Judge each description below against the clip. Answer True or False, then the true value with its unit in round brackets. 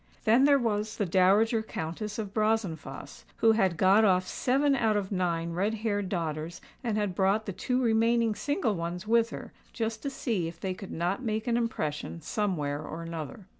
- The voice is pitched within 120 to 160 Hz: False (205 Hz)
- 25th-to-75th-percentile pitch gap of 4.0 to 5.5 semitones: True (4.4 semitones)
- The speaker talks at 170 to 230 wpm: True (185 wpm)